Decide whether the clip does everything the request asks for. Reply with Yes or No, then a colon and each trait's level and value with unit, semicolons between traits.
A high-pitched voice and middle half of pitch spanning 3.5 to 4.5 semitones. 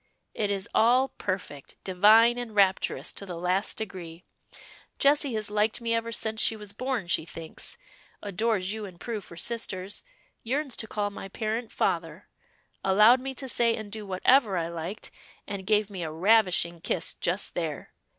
Yes: high, 205 Hz; average, 3.8 semitones